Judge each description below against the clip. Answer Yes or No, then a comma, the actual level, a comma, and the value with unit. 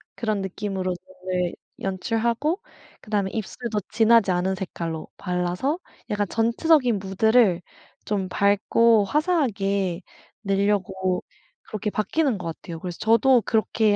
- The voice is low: No, high, 205 Hz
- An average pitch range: Yes, average, 3.6 semitones